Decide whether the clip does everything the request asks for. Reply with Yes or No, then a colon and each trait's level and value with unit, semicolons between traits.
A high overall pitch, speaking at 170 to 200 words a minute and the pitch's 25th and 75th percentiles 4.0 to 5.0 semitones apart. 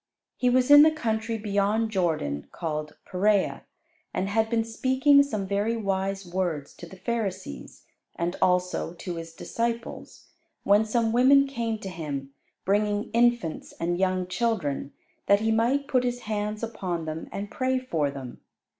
No: high, 205 Hz; average, 155 wpm; average, 4.7 semitones